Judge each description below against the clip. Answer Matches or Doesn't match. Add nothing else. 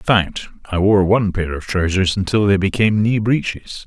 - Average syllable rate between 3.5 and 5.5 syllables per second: Matches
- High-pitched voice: Doesn't match